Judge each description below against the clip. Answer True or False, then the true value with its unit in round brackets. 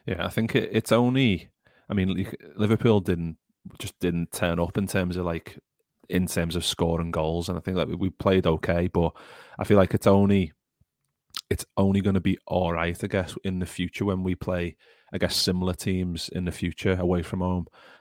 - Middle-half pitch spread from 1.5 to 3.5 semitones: True (2.4 semitones)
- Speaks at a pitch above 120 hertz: False (90 Hz)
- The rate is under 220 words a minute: True (200 wpm)